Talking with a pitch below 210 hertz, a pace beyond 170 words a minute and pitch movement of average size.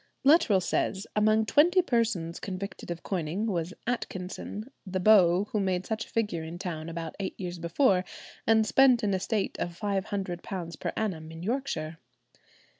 No: high, 190 Hz; average, 155 wpm; average, 4.1 semitones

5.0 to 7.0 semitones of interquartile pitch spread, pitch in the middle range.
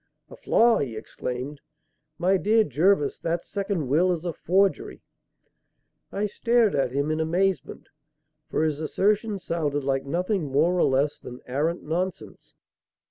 Yes: wide, 5.4 semitones; medium, 165 Hz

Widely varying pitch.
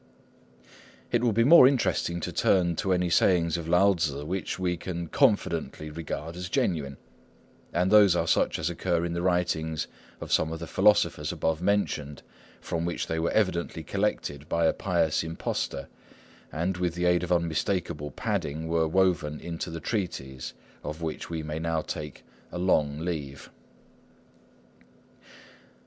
No: narrow, 2.4 semitones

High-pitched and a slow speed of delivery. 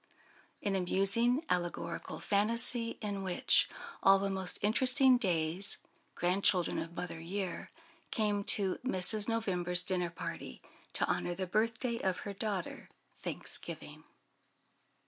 Yes: high, 195 Hz; slow, 105 wpm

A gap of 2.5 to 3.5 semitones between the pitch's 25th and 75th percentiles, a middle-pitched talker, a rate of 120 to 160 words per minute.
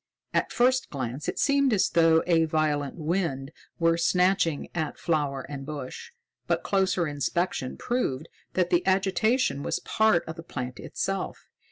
No: average, 4.7 semitones; medium, 165 Hz; average, 150 wpm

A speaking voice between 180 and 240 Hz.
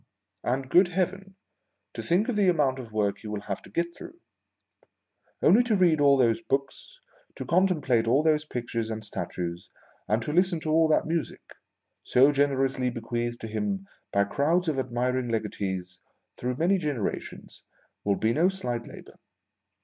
No: low, 135 Hz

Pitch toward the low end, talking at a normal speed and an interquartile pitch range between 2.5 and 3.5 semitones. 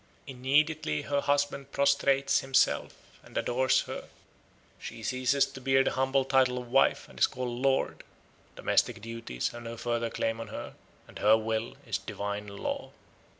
Yes: low, 130 Hz; average, 160 wpm; average, 2.9 semitones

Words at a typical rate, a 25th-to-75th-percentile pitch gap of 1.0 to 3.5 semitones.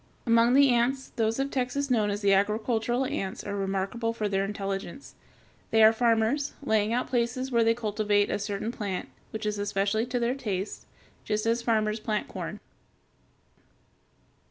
Yes: average, 165 wpm; average, 2.8 semitones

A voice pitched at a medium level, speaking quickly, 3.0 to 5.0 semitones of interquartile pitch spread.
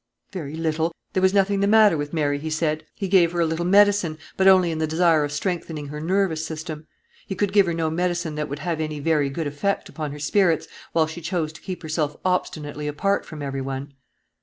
Yes: medium, 160 Hz; fast, 225 wpm; average, 3.3 semitones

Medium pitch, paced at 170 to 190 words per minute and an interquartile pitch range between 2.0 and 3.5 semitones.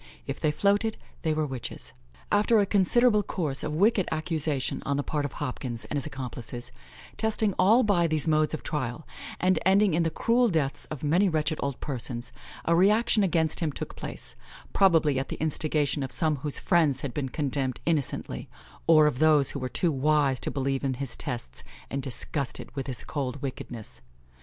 No: medium, 150 Hz; average, 185 wpm; average, 4.3 semitones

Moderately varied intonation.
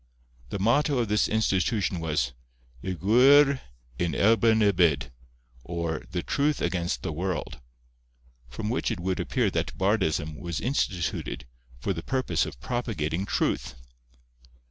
No: wide, 5.8 semitones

